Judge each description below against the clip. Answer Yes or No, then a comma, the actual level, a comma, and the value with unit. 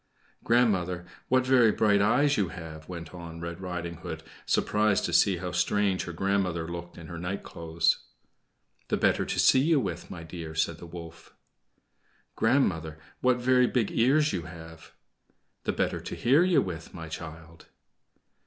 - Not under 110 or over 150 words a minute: No, average, 160 wpm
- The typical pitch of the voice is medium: No, very low, 90 Hz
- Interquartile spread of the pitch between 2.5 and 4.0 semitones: No, average, 5.2 semitones